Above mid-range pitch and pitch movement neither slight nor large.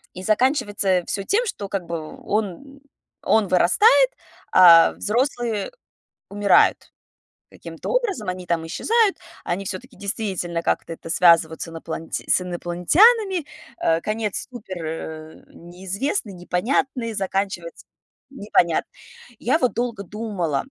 No: high, 200 Hz; wide, 6.1 semitones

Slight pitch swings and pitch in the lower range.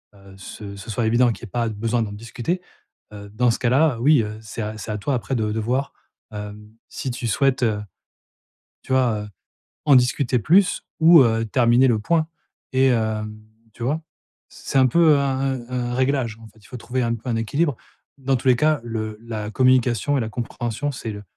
No: average, 3.3 semitones; low, 120 Hz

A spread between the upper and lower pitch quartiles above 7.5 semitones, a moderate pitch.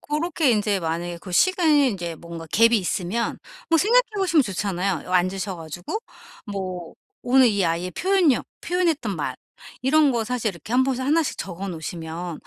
No: wide, 8.6 semitones; high, 205 Hz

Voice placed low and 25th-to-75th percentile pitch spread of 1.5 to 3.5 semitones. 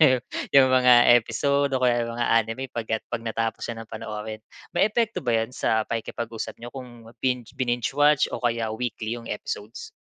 Yes: low, 120 Hz; narrow, 2.5 semitones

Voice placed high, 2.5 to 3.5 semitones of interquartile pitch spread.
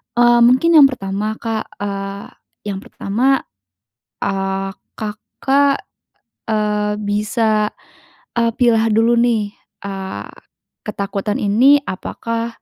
Yes: high, 215 Hz; average, 2.9 semitones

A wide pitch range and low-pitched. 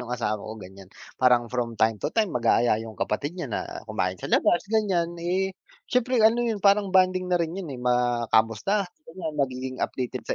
Yes: wide, 8.2 semitones; low, 130 Hz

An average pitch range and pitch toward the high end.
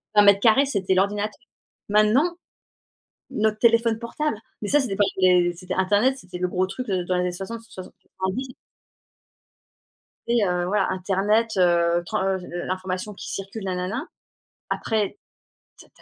Yes: average, 3.5 semitones; high, 200 Hz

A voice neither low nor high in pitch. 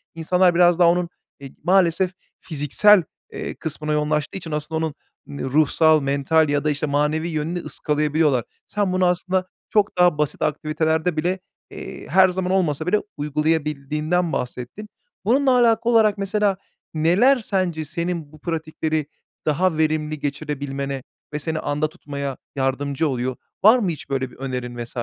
Yes: medium, 155 Hz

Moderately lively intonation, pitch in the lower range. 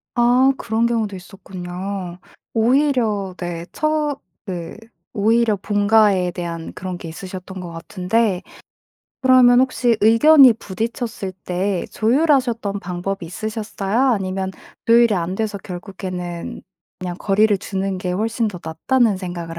No: average, 4.1 semitones; high, 200 Hz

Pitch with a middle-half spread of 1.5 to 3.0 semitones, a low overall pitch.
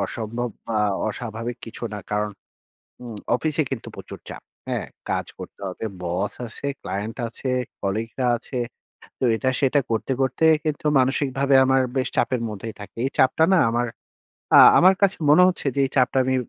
No: average, 3.4 semitones; low, 125 Hz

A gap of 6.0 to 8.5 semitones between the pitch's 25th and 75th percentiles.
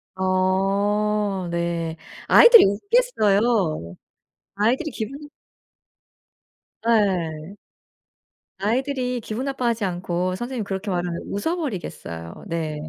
No: average, 5.3 semitones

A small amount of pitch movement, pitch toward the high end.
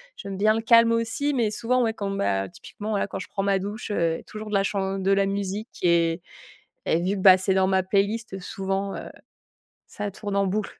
Yes: narrow, 2.1 semitones; high, 200 Hz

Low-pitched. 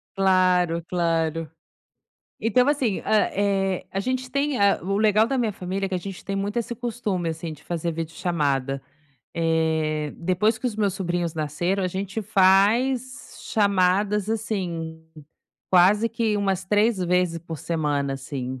No: high, 190 Hz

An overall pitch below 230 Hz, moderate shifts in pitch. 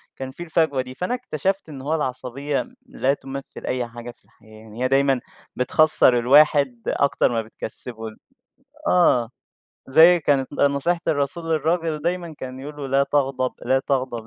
Yes: medium, 140 Hz; average, 3.6 semitones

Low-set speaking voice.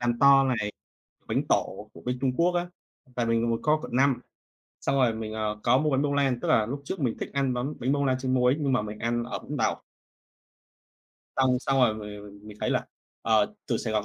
Yes: low, 125 Hz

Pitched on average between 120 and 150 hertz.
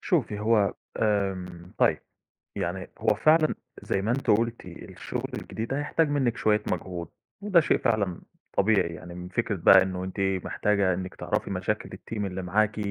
No: low, 105 Hz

